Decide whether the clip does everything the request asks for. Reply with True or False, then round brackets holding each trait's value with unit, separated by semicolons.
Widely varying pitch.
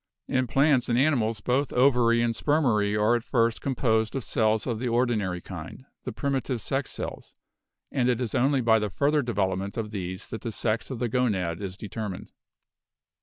False (3.4 semitones)